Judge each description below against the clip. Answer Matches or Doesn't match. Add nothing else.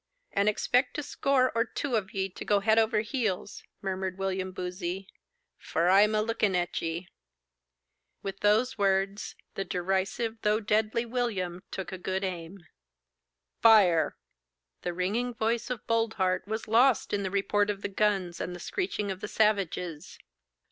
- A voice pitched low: Doesn't match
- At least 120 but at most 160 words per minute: Matches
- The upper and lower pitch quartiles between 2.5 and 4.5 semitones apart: Matches